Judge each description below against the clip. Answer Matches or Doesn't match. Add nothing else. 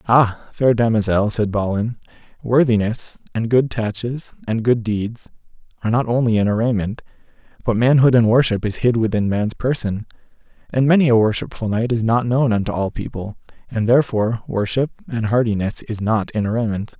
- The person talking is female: Doesn't match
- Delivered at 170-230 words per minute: Doesn't match